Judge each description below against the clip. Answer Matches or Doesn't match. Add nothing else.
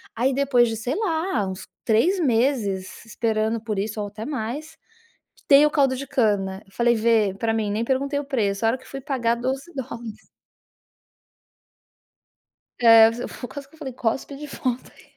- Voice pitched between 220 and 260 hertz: Matches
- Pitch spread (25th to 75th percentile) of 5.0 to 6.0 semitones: Doesn't match